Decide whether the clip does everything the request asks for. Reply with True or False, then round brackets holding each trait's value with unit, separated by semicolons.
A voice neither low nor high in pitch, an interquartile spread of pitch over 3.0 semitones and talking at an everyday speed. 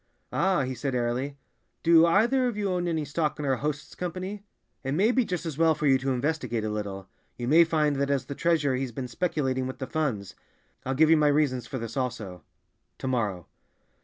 False (145 Hz; 4.4 semitones; 210 wpm)